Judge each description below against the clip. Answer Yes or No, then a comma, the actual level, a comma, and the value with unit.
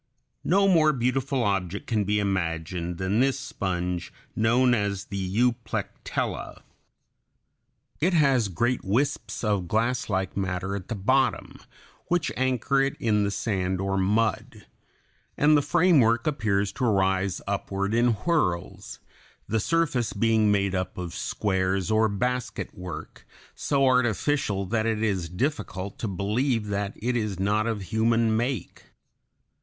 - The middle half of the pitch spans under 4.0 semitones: No, average, 4.5 semitones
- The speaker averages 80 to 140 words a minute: Yes, slow, 135 wpm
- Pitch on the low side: Yes, low, 110 Hz